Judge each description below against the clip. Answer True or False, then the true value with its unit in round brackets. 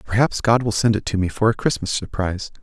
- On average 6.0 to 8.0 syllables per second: True (6.2 syllables/s)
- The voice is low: True (105 Hz)